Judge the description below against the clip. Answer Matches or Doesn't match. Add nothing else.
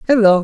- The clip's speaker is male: Doesn't match